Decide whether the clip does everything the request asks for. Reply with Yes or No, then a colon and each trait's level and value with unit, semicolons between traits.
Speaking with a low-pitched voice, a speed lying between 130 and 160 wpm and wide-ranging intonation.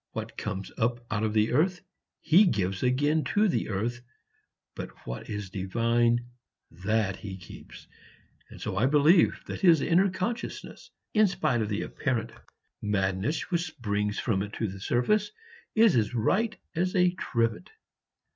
Yes: low, 120 Hz; average, 155 wpm; wide, 8.5 semitones